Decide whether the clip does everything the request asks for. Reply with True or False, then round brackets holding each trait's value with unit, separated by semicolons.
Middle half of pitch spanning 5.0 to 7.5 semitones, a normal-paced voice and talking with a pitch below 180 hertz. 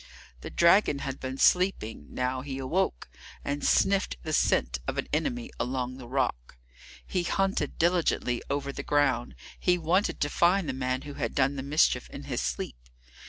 True (5.3 semitones; 170 wpm; 140 Hz)